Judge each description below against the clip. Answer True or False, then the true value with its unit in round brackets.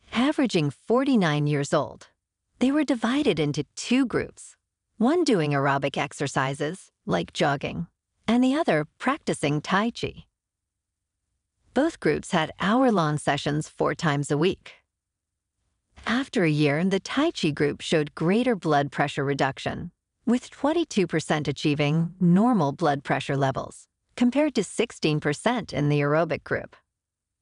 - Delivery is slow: True (125 wpm)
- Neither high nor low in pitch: True (155 Hz)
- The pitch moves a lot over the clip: True (8.1 semitones)